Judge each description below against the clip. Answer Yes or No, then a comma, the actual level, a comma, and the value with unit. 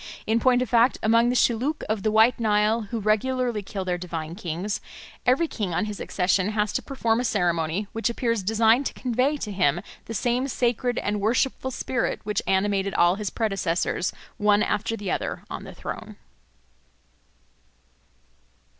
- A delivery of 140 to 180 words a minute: Yes, average, 165 wpm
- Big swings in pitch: No, average, 3.5 semitones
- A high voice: Yes, high, 215 Hz